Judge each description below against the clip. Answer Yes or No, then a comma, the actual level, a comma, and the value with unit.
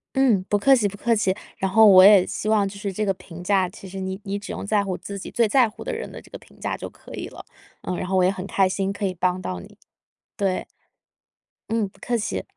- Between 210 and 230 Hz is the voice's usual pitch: No, high, 195 Hz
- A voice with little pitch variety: Yes, narrow, 2.1 semitones